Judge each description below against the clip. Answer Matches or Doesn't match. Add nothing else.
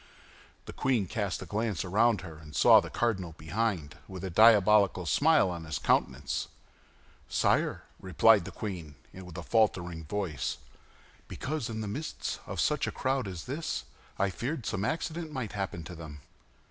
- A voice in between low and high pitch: Doesn't match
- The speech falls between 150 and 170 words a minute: Matches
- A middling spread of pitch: Matches